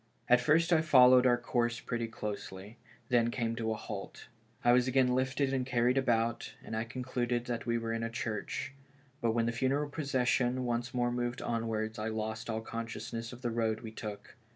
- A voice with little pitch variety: Yes, narrow, 1.8 semitones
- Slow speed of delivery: No, average, 190 wpm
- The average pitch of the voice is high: No, low, 120 Hz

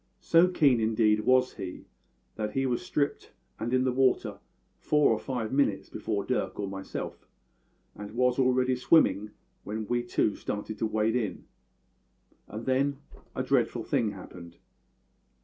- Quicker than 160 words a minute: No, average, 150 wpm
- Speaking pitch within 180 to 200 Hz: No, low, 120 Hz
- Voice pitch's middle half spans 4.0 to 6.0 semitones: No, average, 3.4 semitones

